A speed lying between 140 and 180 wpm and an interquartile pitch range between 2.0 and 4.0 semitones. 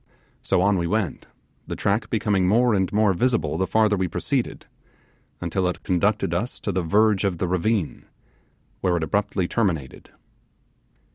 Yes: average, 155 wpm; average, 3.1 semitones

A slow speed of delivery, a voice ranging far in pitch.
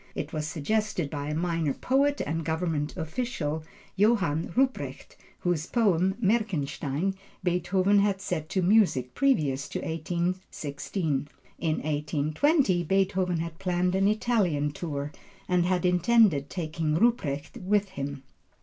No: slow, 120 wpm; average, 4.5 semitones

